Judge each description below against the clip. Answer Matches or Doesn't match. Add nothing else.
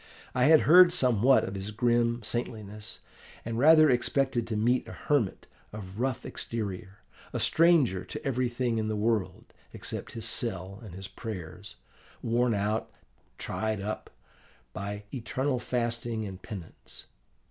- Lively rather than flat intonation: Doesn't match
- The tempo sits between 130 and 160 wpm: Matches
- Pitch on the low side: Matches